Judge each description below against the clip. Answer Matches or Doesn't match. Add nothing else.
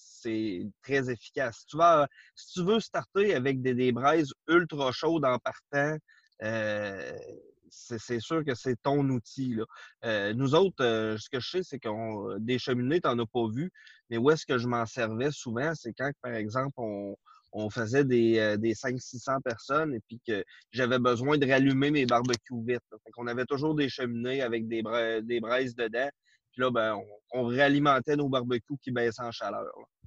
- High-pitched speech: Doesn't match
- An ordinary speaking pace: Matches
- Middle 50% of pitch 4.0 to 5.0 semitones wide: Doesn't match